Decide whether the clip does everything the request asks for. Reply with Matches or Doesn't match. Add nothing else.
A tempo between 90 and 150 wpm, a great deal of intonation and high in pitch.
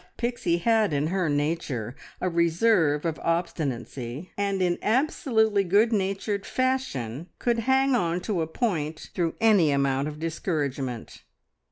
Doesn't match